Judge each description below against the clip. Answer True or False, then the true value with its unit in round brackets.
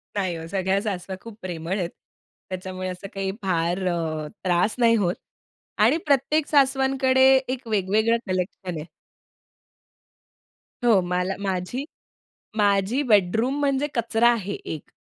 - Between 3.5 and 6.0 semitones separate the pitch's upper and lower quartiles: True (4.6 semitones)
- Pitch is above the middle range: True (200 Hz)